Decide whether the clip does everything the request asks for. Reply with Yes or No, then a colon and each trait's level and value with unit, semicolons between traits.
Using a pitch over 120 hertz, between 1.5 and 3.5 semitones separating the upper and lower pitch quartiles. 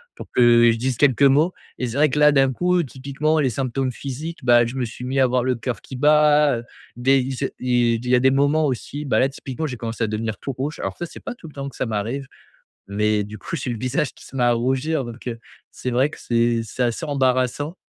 Yes: low, 130 Hz; average, 3.0 semitones